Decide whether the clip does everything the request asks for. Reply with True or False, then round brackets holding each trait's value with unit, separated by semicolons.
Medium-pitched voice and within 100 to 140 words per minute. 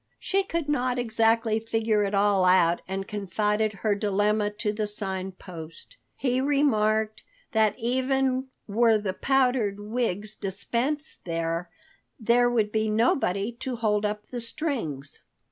False (215 Hz; 135 wpm)